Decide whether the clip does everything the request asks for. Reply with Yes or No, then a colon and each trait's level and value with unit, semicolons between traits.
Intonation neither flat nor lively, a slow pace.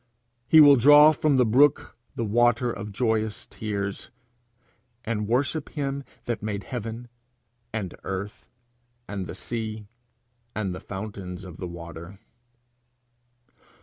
Yes: average, 3.8 semitones; slow, 115 wpm